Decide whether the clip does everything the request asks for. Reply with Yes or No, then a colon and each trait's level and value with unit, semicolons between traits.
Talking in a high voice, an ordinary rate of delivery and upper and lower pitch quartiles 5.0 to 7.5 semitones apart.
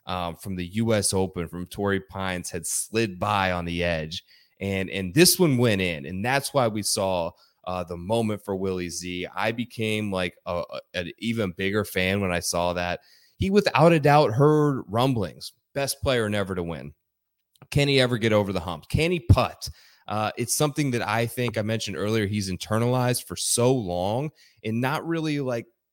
No: low, 105 Hz; average, 190 wpm; wide, 5.4 semitones